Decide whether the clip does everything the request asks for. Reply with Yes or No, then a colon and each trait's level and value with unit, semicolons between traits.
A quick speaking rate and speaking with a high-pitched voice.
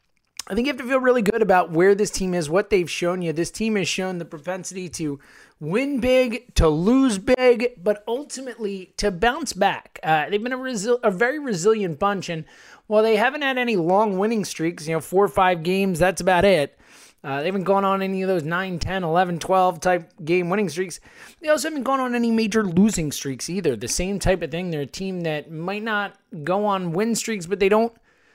Yes: fast, 220 wpm; high, 195 Hz